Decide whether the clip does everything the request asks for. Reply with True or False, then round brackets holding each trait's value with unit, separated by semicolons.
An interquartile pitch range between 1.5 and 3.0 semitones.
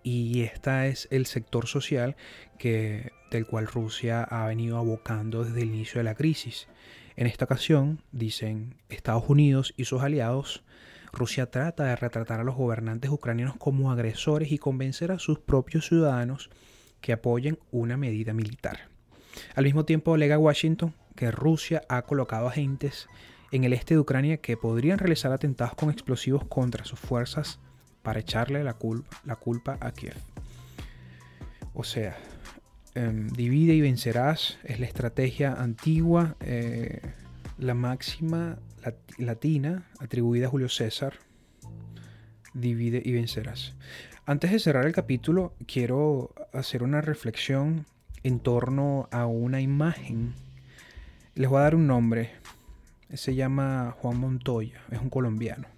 False (3.5 semitones)